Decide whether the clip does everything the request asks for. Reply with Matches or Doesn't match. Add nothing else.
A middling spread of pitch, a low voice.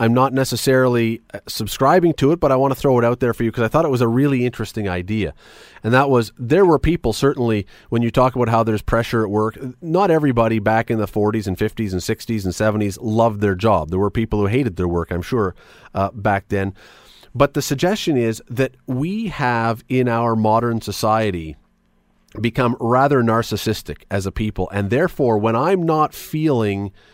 Matches